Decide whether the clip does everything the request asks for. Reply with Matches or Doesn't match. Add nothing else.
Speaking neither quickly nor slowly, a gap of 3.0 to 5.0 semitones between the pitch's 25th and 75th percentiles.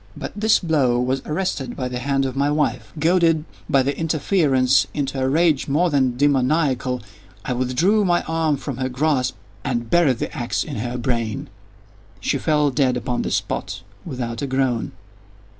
Matches